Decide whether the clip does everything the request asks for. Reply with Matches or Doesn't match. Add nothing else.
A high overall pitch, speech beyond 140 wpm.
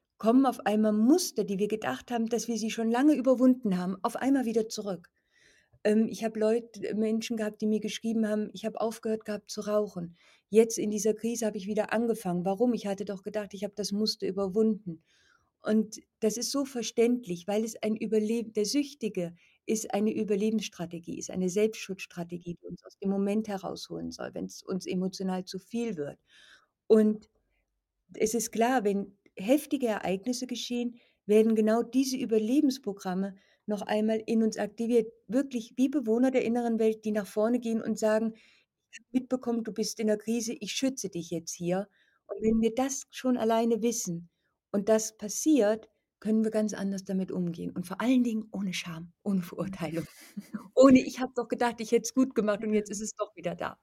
Matches